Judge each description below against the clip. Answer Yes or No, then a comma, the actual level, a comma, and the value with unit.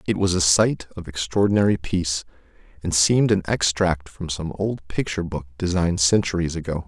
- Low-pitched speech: Yes, very low, 85 Hz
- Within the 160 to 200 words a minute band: Yes, average, 165 wpm